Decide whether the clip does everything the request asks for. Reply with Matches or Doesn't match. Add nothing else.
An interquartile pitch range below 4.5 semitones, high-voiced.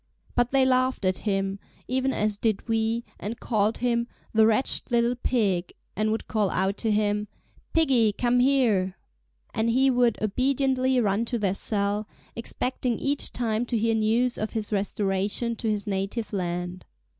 Matches